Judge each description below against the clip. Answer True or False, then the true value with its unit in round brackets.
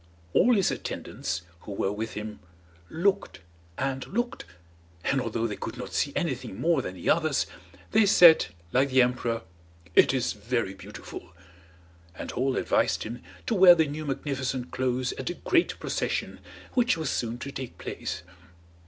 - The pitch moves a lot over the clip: True (5.8 semitones)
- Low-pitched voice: True (130 Hz)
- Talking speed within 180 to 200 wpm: False (160 wpm)